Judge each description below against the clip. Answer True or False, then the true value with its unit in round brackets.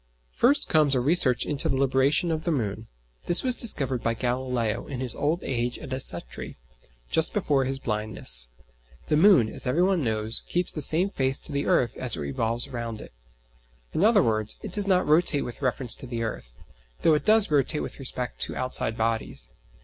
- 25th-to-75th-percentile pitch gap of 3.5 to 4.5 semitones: False (5.2 semitones)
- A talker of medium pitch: False (130 Hz)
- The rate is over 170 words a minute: True (195 wpm)